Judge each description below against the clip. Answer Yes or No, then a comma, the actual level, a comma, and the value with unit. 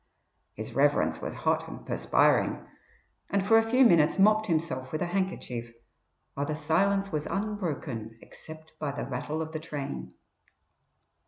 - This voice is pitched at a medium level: Yes, medium, 160 Hz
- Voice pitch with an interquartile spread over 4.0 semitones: Yes, wide, 5.6 semitones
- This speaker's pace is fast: No, average, 150 wpm